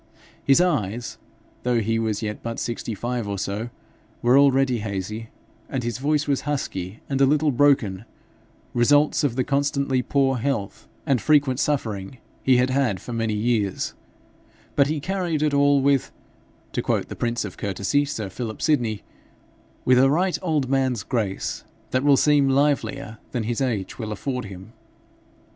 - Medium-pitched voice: No, low, 125 Hz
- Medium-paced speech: Yes, average, 160 wpm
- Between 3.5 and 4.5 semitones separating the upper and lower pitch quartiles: Yes, average, 4.2 semitones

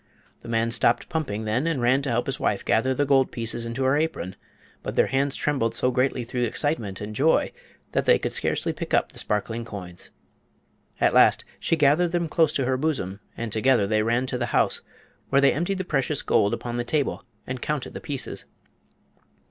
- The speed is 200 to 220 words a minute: Yes, fast, 205 wpm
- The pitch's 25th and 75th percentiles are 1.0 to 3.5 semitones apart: No, average, 3.9 semitones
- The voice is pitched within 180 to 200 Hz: No, low, 130 Hz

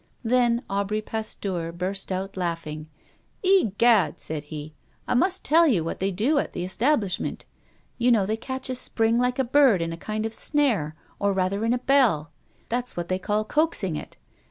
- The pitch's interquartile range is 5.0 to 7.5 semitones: Yes, wide, 5.4 semitones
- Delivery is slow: No, average, 180 wpm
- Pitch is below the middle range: No, high, 215 Hz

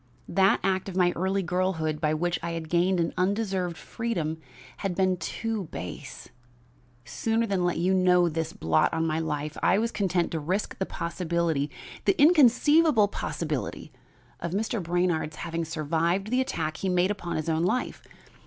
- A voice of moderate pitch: Yes, medium, 175 Hz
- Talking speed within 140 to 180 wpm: Yes, average, 170 wpm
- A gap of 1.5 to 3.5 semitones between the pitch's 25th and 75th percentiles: Yes, average, 3.2 semitones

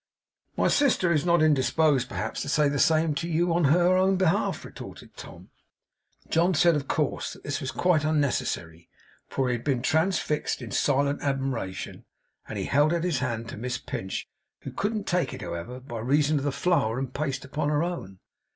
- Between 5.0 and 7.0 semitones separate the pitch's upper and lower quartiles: No, average, 4.5 semitones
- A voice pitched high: No, medium, 145 Hz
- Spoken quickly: No, average, 190 wpm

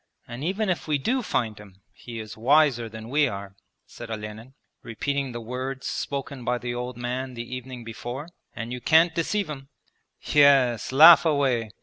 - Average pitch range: Yes, average, 3.5 semitones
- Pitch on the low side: Yes, low, 125 Hz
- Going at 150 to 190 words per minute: Yes, average, 170 wpm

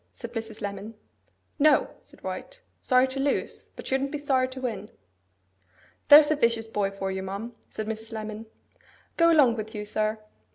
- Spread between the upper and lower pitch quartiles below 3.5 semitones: No, average, 4.0 semitones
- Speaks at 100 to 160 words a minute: No, average, 170 wpm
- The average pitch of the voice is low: No, high, 225 Hz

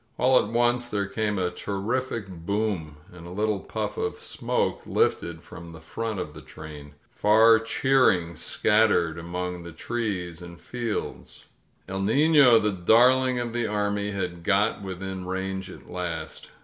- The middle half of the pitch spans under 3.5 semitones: No, average, 4.4 semitones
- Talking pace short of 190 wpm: Yes, average, 155 wpm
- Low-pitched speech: Yes, low, 100 Hz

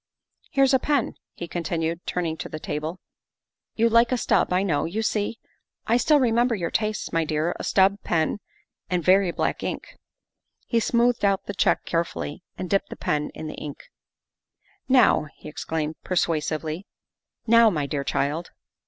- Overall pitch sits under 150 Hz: No, medium, 180 Hz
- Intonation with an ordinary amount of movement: No, wide, 6.0 semitones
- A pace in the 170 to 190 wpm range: Yes, average, 185 wpm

